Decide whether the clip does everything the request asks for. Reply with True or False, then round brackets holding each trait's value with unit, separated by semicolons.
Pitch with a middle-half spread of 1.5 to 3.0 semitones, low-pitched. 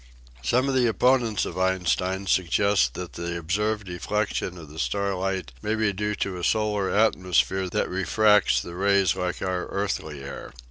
True (2.7 semitones; 95 Hz)